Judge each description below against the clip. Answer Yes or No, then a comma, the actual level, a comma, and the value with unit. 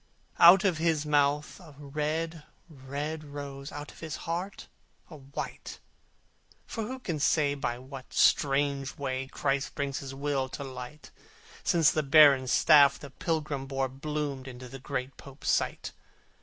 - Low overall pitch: No, medium, 145 Hz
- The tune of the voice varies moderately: No, narrow, 2.2 semitones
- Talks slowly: No, average, 150 wpm